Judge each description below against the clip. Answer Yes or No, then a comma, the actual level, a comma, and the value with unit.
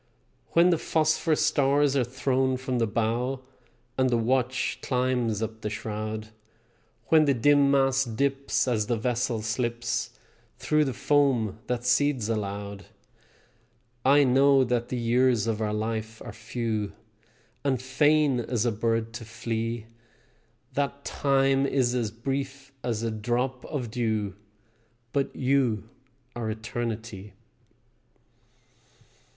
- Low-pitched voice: Yes, low, 120 Hz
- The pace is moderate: No, slow, 125 wpm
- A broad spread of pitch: No, average, 3.3 semitones